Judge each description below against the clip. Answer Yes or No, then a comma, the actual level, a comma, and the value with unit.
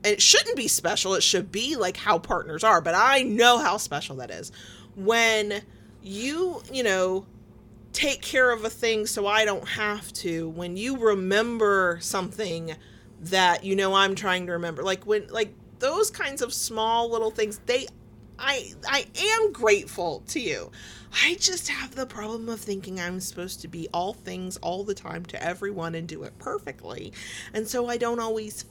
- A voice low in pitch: No, high, 210 Hz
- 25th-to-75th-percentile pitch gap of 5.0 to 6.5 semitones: No, average, 4.0 semitones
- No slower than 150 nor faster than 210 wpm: Yes, average, 180 wpm